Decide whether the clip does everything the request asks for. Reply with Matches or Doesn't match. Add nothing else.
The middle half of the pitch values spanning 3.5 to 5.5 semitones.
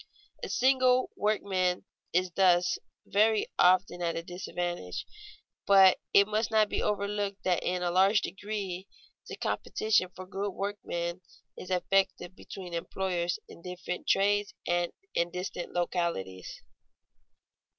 Doesn't match